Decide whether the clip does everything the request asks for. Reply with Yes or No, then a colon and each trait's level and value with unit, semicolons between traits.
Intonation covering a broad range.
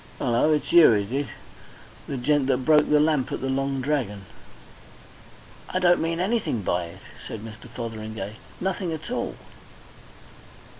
Yes: wide, 5.7 semitones